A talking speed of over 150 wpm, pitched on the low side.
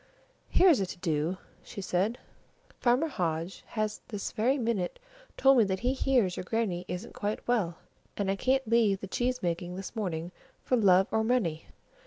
No: average, 175 wpm; high, 205 Hz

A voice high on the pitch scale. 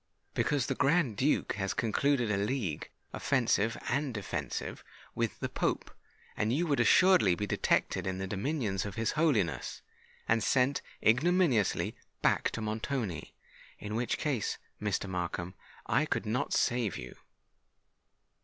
No: low, 115 Hz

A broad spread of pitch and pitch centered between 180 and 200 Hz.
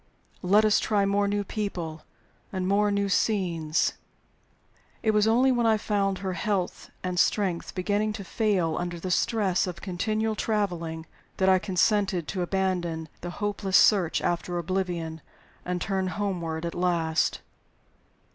No: average, 2.9 semitones; high, 190 Hz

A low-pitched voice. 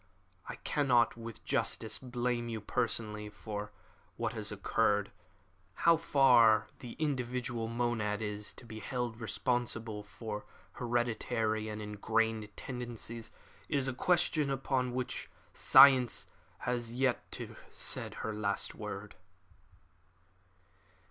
Yes: low, 120 Hz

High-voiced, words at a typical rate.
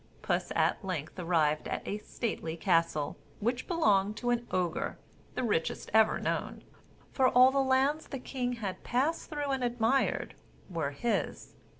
Yes: high, 230 Hz; average, 155 wpm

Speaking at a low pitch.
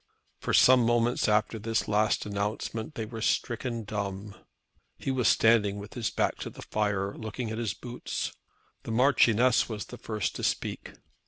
Yes: low, 110 Hz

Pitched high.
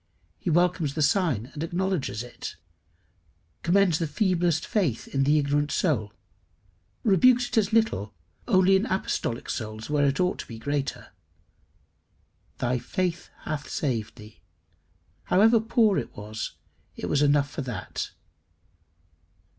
No: medium, 150 Hz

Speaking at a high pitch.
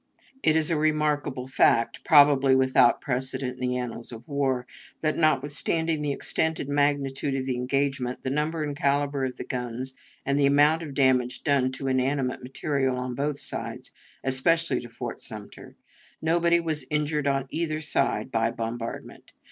No: medium, 140 Hz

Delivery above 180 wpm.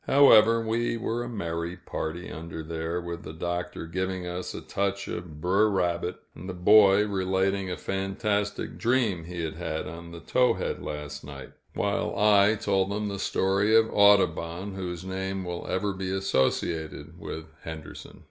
No: average, 160 wpm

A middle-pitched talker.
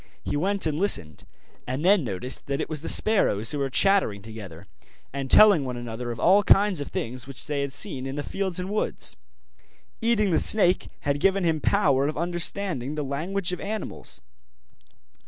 Yes: medium, 150 Hz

